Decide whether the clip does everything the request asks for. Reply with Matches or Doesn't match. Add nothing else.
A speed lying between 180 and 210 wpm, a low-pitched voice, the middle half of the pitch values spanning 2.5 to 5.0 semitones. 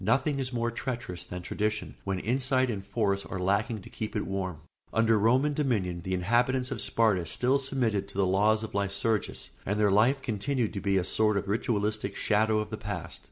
Matches